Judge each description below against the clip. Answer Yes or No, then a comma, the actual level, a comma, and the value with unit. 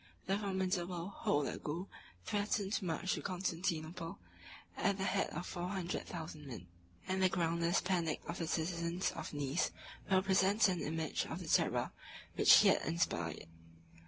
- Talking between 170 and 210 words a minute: No, average, 155 wpm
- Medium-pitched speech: Yes, medium, 175 Hz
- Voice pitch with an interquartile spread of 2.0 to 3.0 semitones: Yes, narrow, 2.6 semitones